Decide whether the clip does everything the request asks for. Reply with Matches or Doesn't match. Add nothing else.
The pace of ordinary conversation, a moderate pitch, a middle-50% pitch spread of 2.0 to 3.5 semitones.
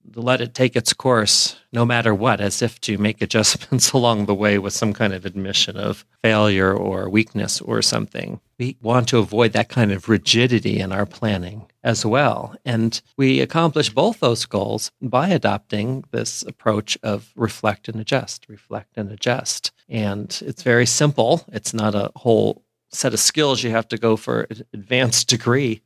Doesn't match